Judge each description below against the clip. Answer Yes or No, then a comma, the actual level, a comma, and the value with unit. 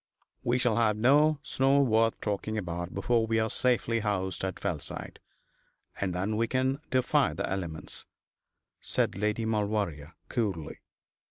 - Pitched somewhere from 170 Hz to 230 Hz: No, low, 110 Hz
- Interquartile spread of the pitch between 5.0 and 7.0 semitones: No, average, 3.8 semitones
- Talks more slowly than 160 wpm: Yes, average, 140 wpm